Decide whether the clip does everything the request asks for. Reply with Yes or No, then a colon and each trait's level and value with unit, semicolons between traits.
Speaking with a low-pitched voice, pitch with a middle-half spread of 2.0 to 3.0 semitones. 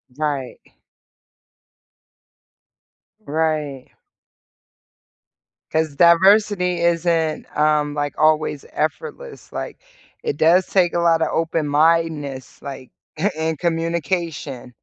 No: medium, 160 Hz; narrow, 2.5 semitones